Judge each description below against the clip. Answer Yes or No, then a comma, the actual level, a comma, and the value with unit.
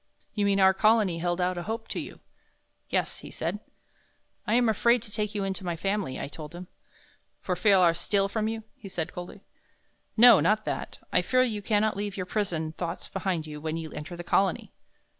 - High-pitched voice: Yes, high, 195 Hz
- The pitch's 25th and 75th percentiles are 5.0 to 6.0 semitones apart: No, average, 3.5 semitones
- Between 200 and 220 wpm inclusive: Yes, fast, 205 wpm